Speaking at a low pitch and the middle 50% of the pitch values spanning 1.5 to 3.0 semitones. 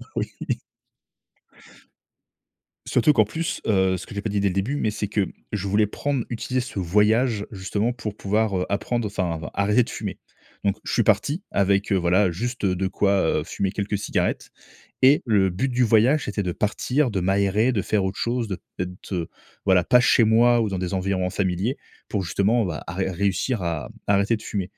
No: low, 100 Hz; average, 3.4 semitones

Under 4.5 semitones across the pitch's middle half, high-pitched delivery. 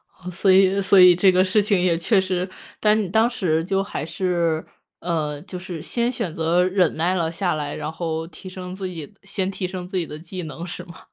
No: narrow, 2.4 semitones; medium, 180 Hz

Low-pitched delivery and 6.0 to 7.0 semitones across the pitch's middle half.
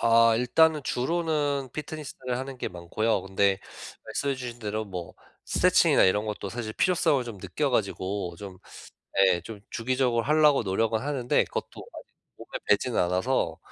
No: low, 115 Hz; average, 5.3 semitones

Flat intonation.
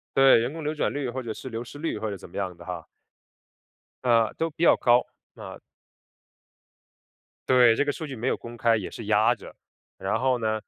No: average, 3.6 semitones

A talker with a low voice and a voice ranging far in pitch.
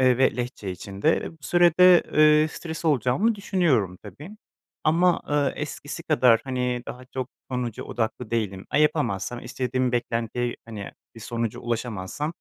No: low, 125 Hz; average, 4.8 semitones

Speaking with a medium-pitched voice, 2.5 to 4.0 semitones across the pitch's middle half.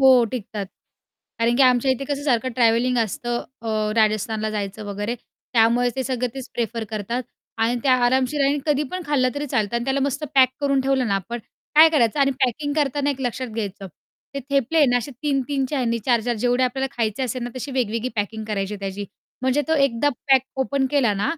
No: high, 245 Hz; average, 3.3 semitones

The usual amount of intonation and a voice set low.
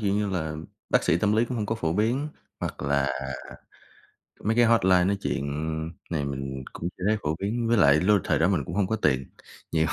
No: wide, 6.0 semitones; very low, 95 Hz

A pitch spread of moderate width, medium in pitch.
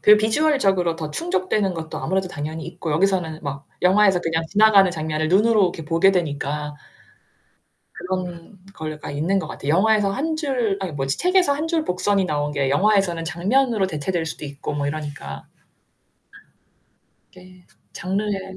Yes: average, 4.6 semitones; medium, 180 Hz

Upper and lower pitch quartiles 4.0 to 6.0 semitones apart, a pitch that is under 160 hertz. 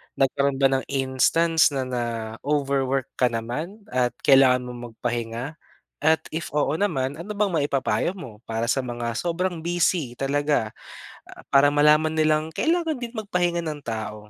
Yes: average, 4.8 semitones; medium, 140 Hz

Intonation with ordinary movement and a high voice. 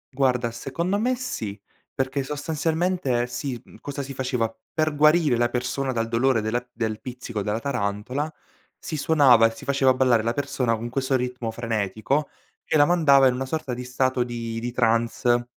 No: average, 3.2 semitones; low, 125 Hz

